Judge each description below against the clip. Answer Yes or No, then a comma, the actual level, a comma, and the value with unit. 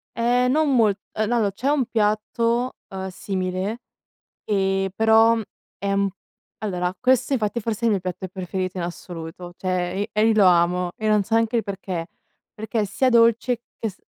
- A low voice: No, high, 210 Hz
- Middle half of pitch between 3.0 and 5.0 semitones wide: Yes, average, 3.7 semitones